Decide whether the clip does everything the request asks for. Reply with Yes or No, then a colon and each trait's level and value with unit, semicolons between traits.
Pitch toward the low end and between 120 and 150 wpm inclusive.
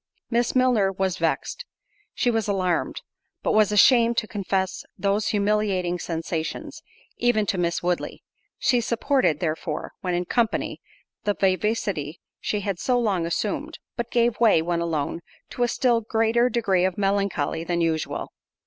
No: high, 200 Hz; average, 140 wpm